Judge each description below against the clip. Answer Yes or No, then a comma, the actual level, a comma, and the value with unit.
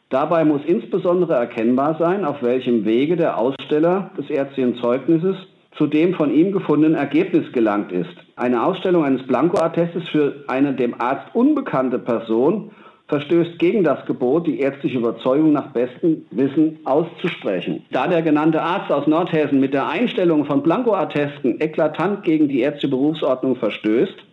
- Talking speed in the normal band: Yes, average, 145 wpm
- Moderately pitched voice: Yes, medium, 155 Hz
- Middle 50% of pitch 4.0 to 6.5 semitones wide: Yes, average, 5.0 semitones